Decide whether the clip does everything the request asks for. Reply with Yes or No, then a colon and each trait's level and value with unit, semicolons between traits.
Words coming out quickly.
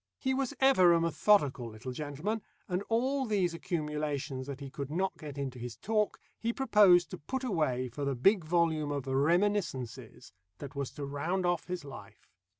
No: average, 175 wpm